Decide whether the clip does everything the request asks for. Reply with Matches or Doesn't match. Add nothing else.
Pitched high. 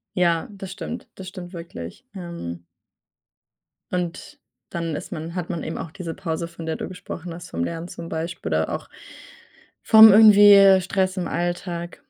Doesn't match